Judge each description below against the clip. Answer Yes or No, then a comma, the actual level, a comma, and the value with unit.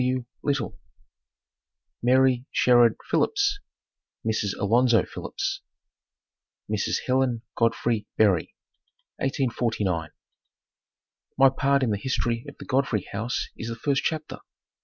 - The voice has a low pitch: Yes, low, 125 Hz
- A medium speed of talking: No, slow, 105 wpm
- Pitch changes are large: No, average, 3.0 semitones